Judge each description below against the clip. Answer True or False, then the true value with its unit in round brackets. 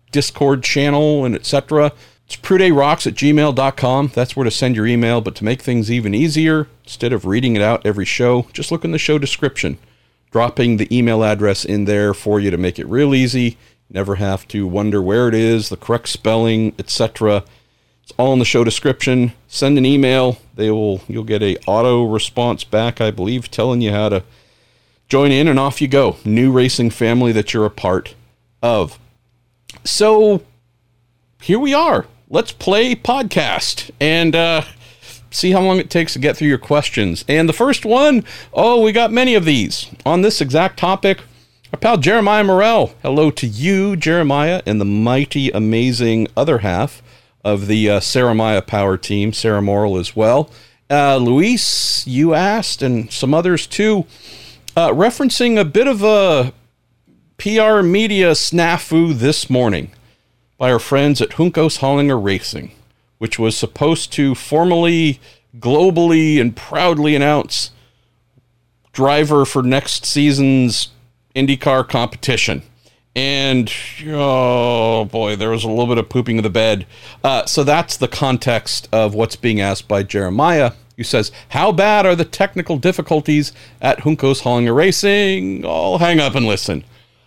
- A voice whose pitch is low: True (125 Hz)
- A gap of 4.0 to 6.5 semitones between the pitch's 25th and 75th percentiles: True (5.2 semitones)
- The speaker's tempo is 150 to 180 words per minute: True (160 wpm)